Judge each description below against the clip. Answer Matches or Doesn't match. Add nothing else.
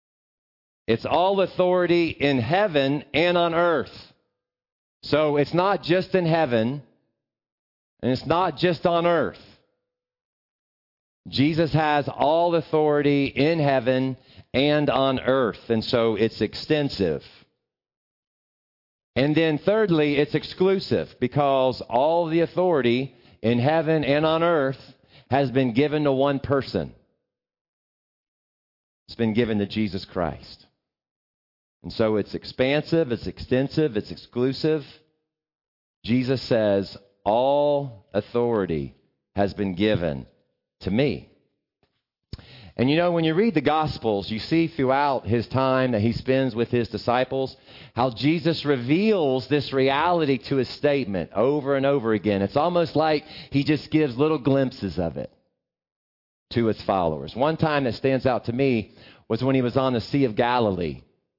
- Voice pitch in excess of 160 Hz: Doesn't match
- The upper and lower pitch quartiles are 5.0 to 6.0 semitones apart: Matches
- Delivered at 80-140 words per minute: Matches